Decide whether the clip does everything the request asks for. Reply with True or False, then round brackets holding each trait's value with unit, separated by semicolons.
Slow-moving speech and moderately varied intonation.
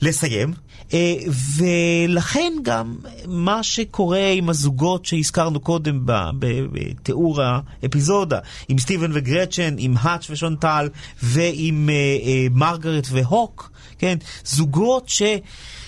True (90 wpm; 4.2 semitones)